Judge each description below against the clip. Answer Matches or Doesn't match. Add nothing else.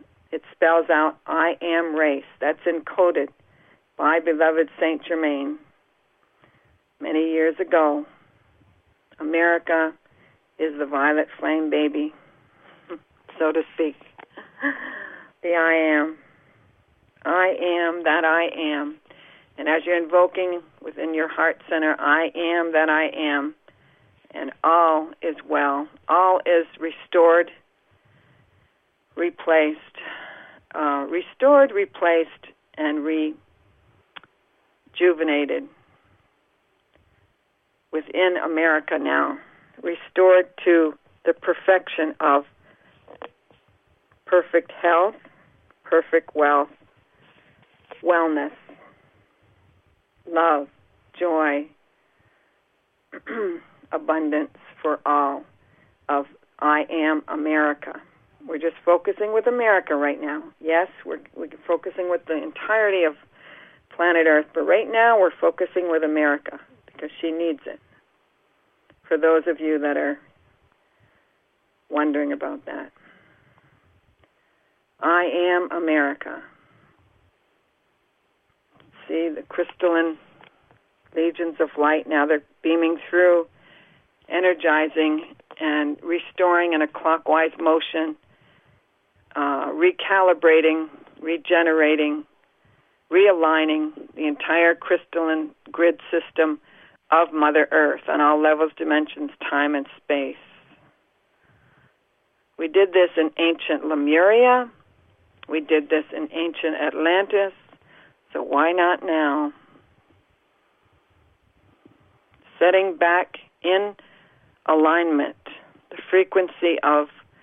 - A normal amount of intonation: Doesn't match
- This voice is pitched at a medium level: Matches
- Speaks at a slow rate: Matches